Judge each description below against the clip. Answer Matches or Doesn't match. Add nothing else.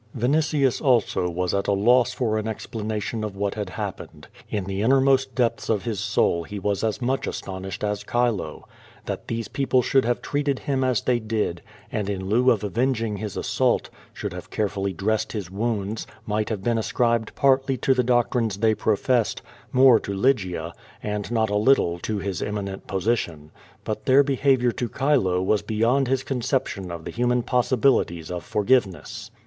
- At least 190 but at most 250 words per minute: Doesn't match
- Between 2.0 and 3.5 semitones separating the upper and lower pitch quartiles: Doesn't match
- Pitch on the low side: Matches